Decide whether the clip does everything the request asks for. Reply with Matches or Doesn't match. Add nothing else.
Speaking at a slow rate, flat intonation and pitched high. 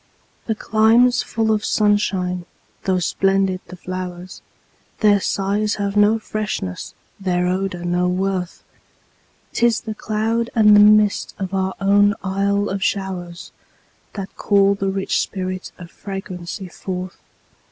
Matches